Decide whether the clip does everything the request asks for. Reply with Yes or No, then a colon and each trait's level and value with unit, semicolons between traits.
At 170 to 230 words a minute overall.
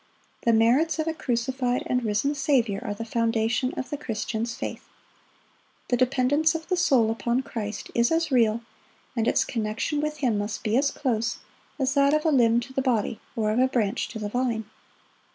Yes: average, 190 wpm